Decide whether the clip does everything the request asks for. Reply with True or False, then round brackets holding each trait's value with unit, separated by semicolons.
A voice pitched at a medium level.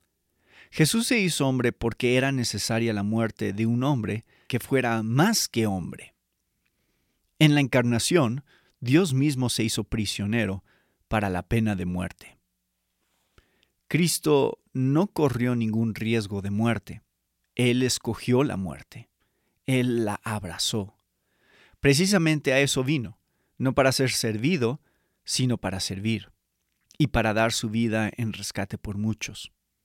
False (115 Hz)